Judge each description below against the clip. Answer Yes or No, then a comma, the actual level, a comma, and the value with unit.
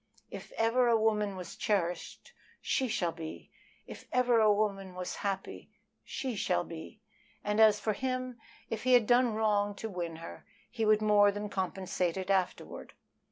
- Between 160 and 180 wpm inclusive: Yes, average, 165 wpm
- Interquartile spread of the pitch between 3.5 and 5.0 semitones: No, average, 3.1 semitones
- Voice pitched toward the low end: No, high, 210 Hz